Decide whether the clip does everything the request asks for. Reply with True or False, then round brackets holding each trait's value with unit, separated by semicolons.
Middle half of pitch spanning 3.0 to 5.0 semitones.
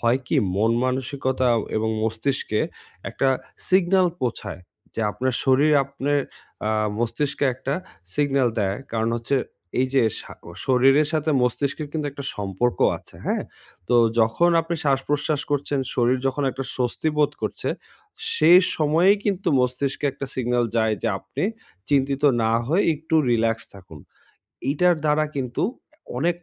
True (3.8 semitones)